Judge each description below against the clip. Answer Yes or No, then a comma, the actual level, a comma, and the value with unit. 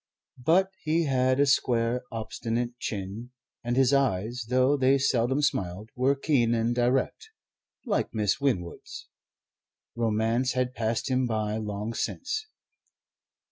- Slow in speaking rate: Yes, slow, 125 wpm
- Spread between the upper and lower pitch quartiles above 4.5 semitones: No, average, 3.1 semitones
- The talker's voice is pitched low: Yes, low, 120 Hz